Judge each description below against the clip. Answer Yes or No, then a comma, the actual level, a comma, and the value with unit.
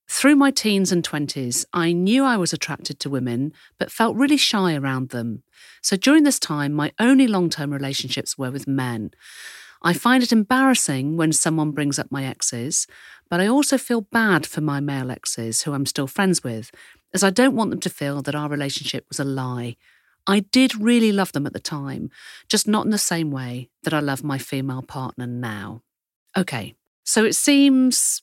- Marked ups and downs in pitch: Yes, wide, 7.9 semitones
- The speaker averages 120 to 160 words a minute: No, average, 195 wpm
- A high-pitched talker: No, medium, 150 Hz